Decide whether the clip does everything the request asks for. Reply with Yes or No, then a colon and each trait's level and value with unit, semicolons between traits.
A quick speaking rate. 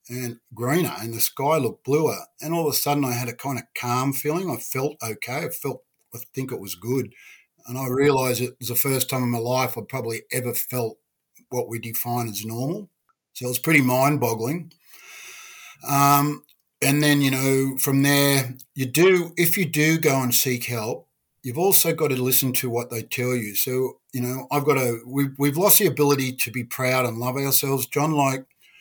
Yes: fast, 210 wpm